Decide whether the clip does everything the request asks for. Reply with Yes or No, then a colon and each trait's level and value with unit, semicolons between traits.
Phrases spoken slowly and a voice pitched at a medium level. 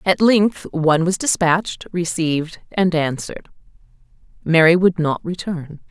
Yes: slow, 120 wpm; medium, 170 Hz